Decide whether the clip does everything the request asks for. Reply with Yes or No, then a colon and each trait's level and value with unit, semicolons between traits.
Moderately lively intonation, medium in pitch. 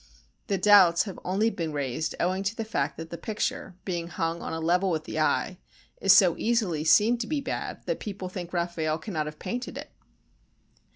Yes: average, 4.2 semitones; medium, 180 Hz